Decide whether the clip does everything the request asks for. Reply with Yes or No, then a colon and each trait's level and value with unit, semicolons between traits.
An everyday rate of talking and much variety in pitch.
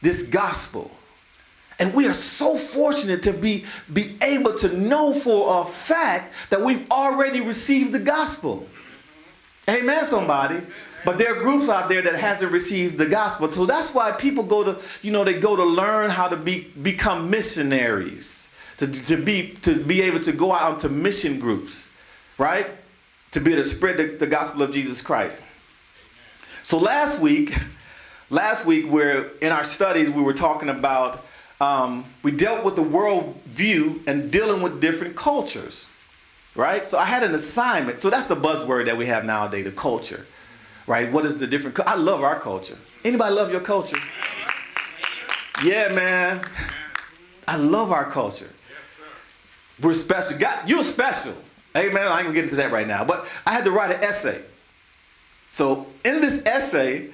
Yes: average, 170 wpm; wide, 7.7 semitones